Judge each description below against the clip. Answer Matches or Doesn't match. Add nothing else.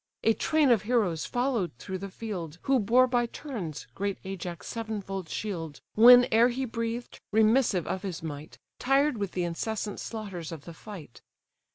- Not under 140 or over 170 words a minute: Matches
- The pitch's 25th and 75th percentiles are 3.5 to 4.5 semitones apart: Doesn't match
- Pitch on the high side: Matches